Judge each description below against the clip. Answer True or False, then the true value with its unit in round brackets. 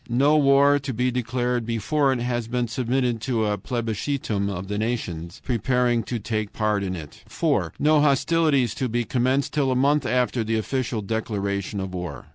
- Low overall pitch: True (120 Hz)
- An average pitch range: True (3.6 semitones)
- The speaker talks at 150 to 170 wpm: False (180 wpm)